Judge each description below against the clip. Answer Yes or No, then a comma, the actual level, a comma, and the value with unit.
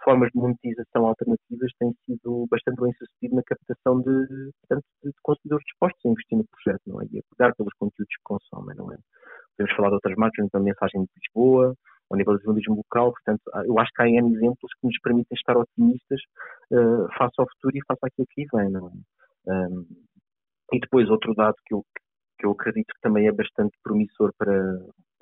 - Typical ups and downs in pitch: Yes, average, 3.3 semitones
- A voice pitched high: No, low, 120 Hz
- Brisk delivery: Yes, fast, 200 wpm